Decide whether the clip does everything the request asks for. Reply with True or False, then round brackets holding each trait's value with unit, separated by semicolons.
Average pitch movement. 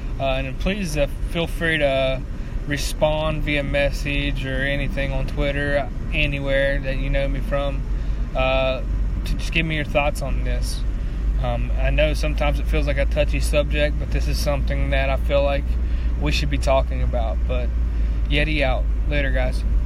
False (6.7 semitones)